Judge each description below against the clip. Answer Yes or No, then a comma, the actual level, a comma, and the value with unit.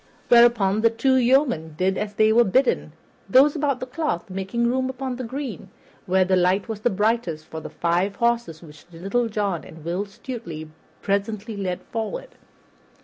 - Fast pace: No, average, 165 wpm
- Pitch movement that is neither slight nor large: Yes, average, 4.7 semitones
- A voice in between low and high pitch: No, high, 210 Hz